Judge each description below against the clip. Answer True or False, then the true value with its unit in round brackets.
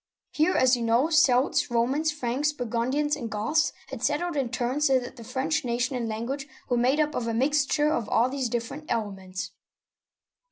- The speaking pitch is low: False (255 Hz)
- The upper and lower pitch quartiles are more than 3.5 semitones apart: True (4.0 semitones)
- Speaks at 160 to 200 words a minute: True (190 wpm)